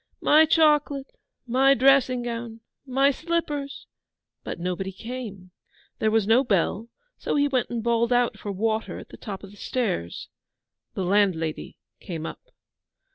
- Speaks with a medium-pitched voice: No, high, 235 Hz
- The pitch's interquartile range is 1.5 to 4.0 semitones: No, average, 5.3 semitones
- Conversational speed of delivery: Yes, average, 145 wpm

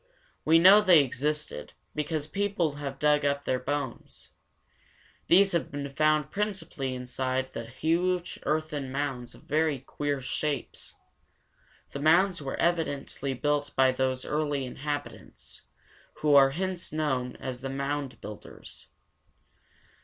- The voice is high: No, medium, 145 Hz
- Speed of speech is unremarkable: No, slow, 125 wpm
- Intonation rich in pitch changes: No, average, 2.8 semitones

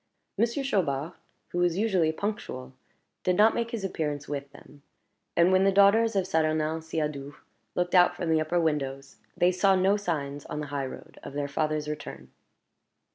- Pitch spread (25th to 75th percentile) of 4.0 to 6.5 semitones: Yes, average, 4.6 semitones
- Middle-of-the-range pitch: Yes, medium, 160 Hz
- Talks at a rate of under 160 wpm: No, average, 175 wpm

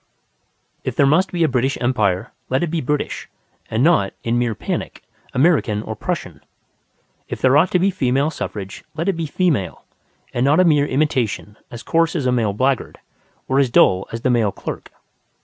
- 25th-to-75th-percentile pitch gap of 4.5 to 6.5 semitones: Yes, wide, 5.4 semitones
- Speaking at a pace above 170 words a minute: Yes, average, 185 wpm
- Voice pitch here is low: Yes, low, 130 Hz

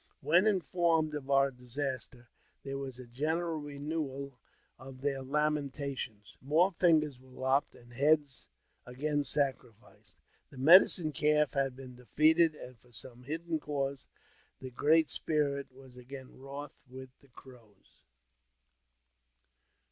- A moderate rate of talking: No, slow, 125 wpm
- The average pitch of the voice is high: No, medium, 140 Hz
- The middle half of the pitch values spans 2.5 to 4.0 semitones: Yes, average, 2.8 semitones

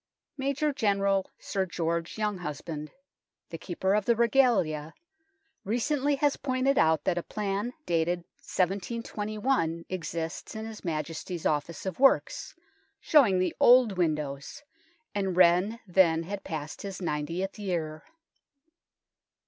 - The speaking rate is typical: No, slow, 115 wpm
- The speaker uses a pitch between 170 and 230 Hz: Yes, high, 190 Hz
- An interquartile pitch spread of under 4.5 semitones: No, average, 5.1 semitones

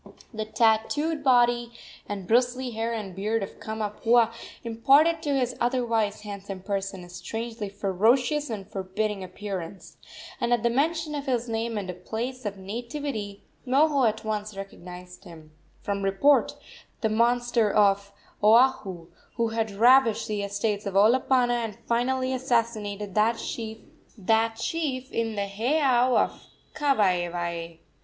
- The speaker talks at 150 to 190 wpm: No, slow, 135 wpm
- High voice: Yes, high, 225 Hz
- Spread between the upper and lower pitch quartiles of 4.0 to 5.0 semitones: No, average, 3.5 semitones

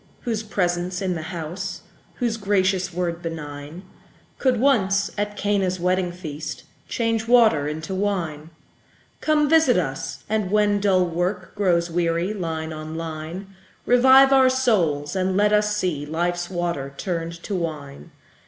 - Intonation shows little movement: No, average, 4.0 semitones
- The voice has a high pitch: No, medium, 180 Hz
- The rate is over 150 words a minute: No, average, 140 wpm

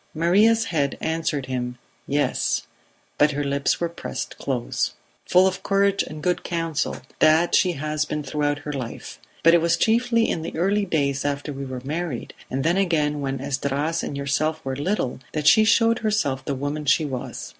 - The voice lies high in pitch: No, medium, 150 Hz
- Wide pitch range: No, average, 3.8 semitones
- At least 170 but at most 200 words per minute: Yes, average, 180 wpm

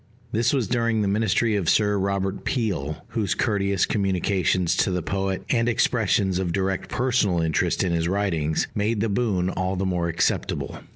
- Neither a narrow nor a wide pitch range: Yes, average, 3.2 semitones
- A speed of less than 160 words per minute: No, average, 170 wpm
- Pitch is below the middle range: Yes, low, 100 Hz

